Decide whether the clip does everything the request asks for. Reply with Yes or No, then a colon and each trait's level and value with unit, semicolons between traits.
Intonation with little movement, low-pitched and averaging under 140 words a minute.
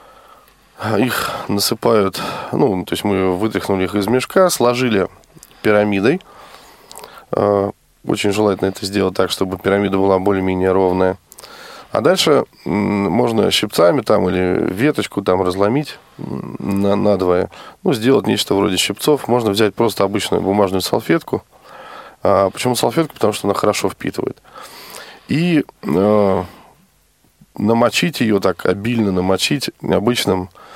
Yes: narrow, 2.2 semitones; low, 100 Hz; average, 115 wpm